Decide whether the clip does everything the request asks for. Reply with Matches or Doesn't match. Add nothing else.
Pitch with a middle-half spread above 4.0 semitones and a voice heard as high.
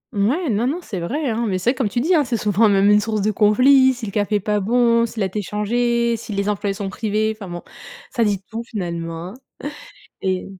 Doesn't match